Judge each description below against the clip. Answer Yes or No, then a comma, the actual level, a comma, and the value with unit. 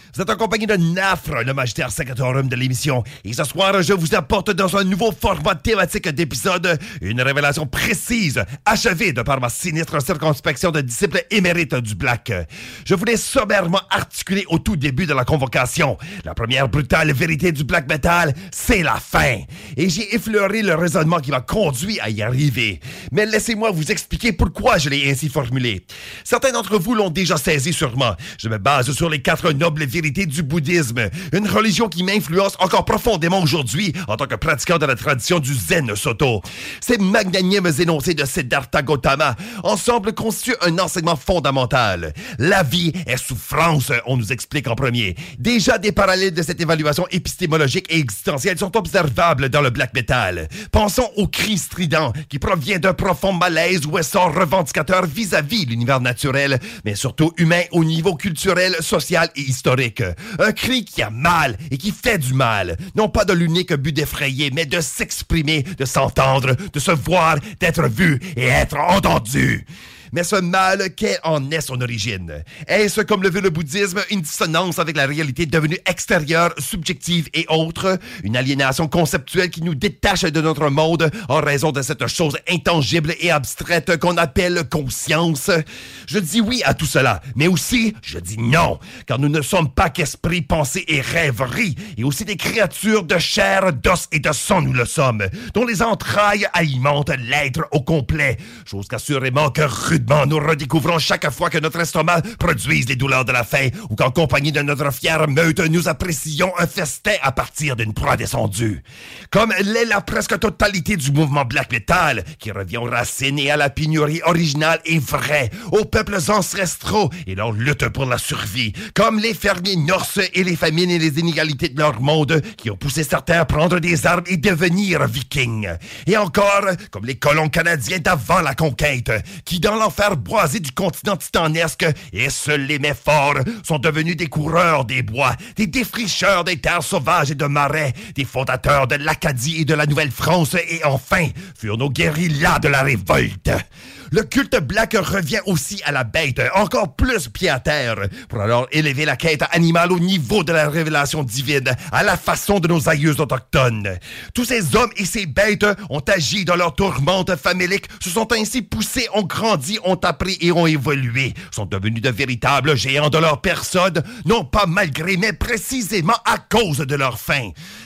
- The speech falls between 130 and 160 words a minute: No, average, 175 wpm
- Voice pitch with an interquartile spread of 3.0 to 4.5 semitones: No, average, 5.0 semitones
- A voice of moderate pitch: Yes, medium, 165 Hz